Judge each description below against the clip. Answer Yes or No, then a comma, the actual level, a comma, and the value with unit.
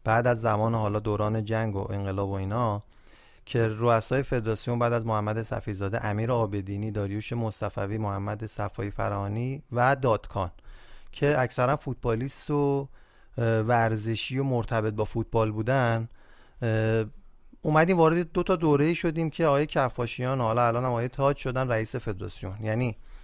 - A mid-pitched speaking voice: No, low, 115 Hz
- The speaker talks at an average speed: Yes, average, 140 wpm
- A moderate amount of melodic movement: Yes, average, 3.1 semitones